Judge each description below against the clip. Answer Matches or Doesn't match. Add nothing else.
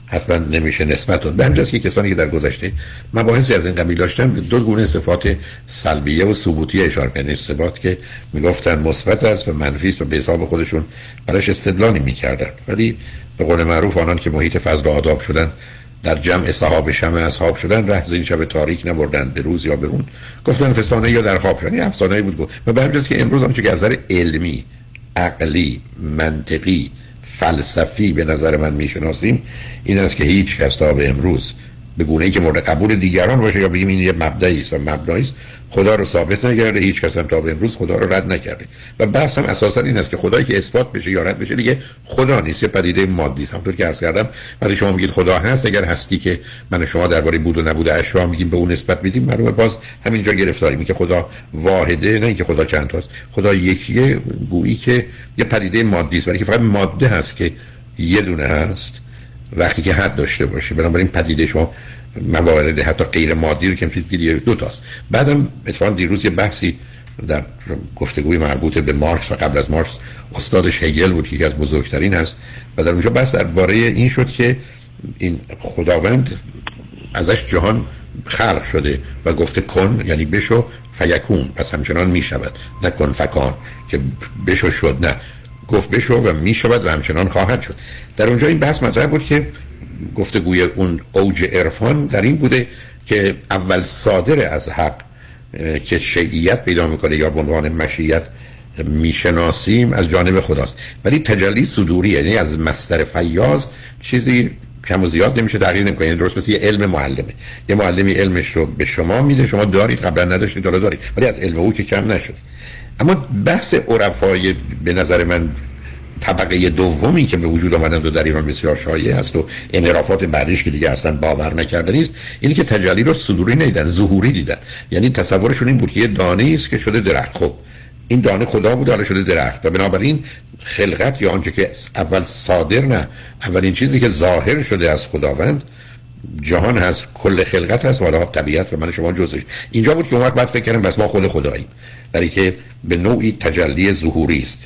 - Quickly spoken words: Matches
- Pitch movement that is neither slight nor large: Doesn't match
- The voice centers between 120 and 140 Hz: Doesn't match